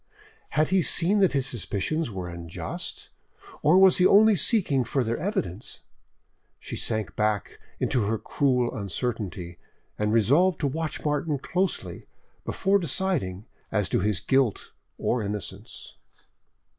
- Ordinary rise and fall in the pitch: No, wide, 8.2 semitones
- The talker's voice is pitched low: Yes, low, 125 Hz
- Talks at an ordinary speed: No, slow, 130 wpm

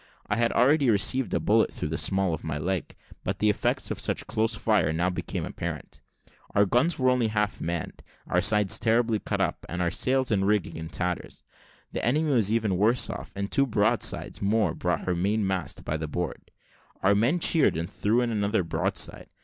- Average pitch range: Yes, average, 4.2 semitones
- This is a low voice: Yes, low, 105 Hz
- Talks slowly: No, average, 200 wpm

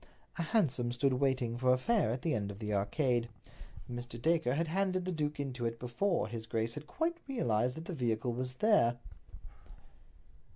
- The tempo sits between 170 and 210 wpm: Yes, average, 180 wpm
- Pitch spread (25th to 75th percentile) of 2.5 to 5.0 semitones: No, wide, 5.5 semitones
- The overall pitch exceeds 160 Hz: No, low, 125 Hz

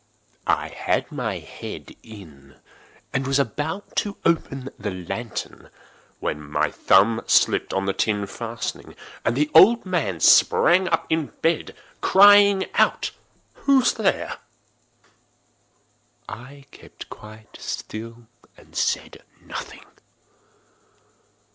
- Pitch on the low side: Yes, low, 125 Hz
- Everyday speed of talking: No, slow, 105 wpm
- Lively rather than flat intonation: Yes, wide, 8.7 semitones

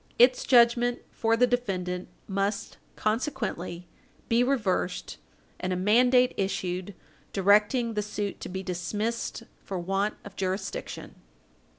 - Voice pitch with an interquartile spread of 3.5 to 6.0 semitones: Yes, average, 4.1 semitones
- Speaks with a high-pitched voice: Yes, high, 210 Hz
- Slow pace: Yes, slow, 115 wpm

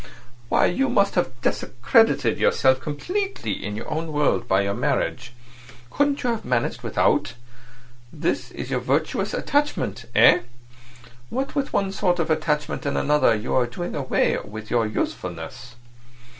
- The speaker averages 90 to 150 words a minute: Yes, average, 145 wpm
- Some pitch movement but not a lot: No, wide, 8.5 semitones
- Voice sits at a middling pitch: Yes, medium, 145 Hz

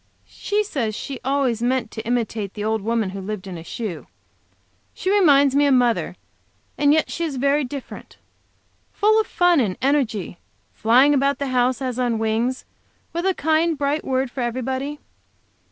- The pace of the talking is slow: No, average, 170 wpm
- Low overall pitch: No, very high, 260 Hz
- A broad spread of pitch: No, average, 4.1 semitones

